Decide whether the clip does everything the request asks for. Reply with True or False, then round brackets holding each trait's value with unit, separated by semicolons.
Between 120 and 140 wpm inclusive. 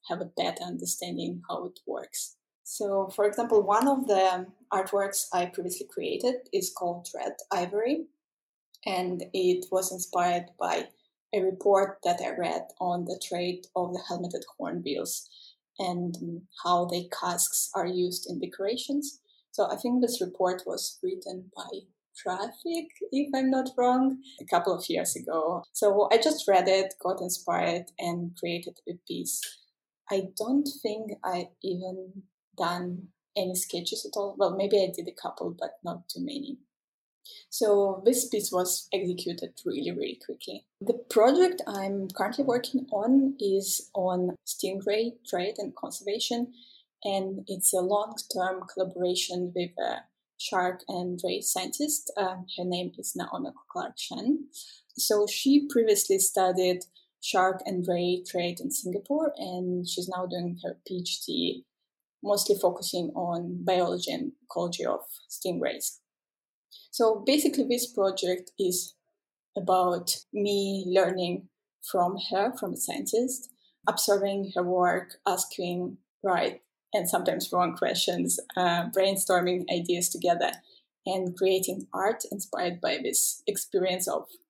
True (135 wpm)